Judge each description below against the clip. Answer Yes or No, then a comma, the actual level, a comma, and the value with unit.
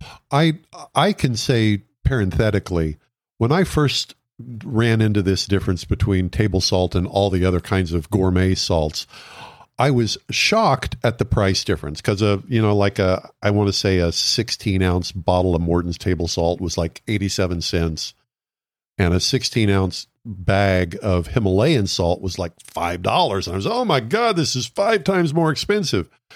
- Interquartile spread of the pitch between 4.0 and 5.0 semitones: Yes, average, 4.5 semitones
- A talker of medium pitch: No, low, 100 Hz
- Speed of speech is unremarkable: Yes, average, 170 wpm